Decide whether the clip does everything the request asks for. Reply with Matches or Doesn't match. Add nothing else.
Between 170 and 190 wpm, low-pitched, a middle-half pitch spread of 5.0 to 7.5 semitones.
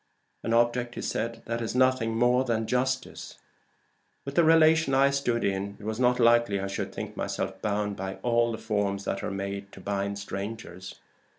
Doesn't match